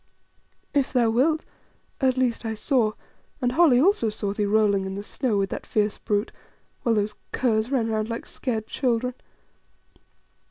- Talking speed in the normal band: Yes, average, 160 wpm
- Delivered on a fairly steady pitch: No, average, 3.3 semitones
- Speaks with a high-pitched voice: Yes, high, 225 Hz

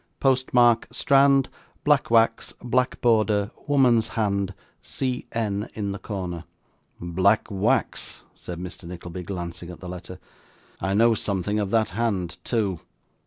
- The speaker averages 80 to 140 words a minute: Yes, slow, 135 wpm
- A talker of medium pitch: No, low, 105 Hz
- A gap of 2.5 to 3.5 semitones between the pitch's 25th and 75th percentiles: No, average, 4.2 semitones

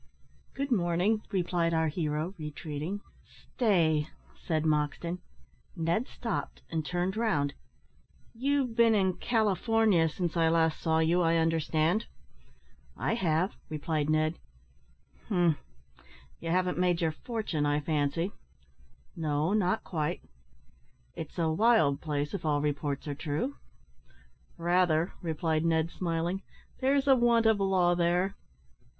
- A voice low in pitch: No, medium, 170 Hz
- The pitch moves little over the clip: No, average, 3.9 semitones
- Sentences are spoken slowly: Yes, slow, 120 wpm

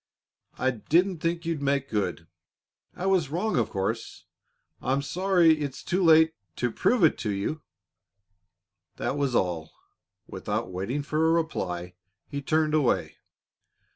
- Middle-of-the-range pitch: Yes, medium, 145 Hz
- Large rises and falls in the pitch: Yes, wide, 6.4 semitones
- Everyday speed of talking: Yes, average, 145 wpm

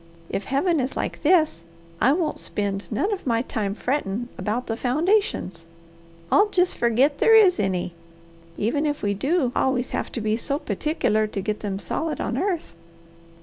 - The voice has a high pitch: Yes, very high, 250 Hz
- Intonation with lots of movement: Yes, wide, 7.0 semitones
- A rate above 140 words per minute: Yes, average, 170 wpm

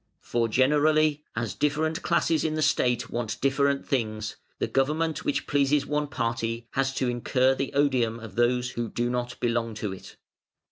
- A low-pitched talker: Yes, low, 130 Hz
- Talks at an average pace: Yes, average, 170 wpm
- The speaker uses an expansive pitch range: No, average, 3.8 semitones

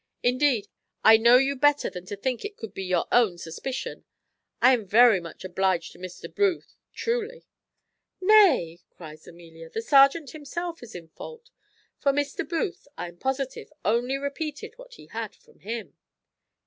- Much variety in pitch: Yes, wide, 8.3 semitones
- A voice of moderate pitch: No, very high, 250 Hz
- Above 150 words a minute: Yes, average, 160 wpm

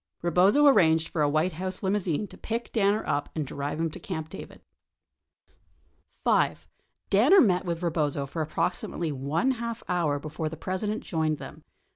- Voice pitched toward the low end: No, medium, 170 Hz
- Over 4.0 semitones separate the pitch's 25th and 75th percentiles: Yes, average, 4.4 semitones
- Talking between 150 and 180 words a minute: Yes, average, 160 wpm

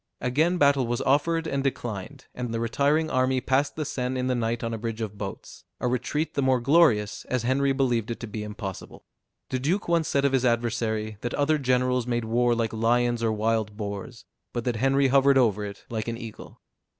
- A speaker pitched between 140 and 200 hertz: No, low, 125 Hz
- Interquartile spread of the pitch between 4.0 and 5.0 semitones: No, average, 3.2 semitones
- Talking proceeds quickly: Yes, fast, 210 wpm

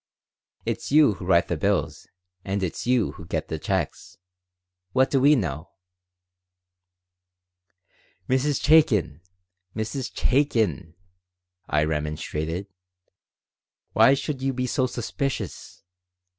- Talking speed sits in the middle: No, slow, 105 wpm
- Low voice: Yes, low, 105 Hz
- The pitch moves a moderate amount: No, wide, 8.0 semitones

